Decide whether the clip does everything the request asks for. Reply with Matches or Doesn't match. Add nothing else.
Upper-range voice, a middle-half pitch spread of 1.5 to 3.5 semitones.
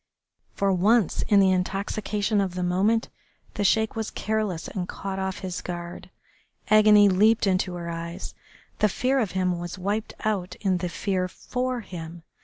Matches